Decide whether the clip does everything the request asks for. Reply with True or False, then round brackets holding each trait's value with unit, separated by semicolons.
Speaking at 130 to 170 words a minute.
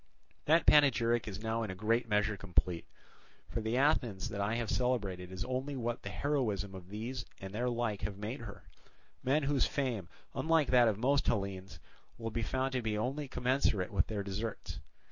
False (185 wpm)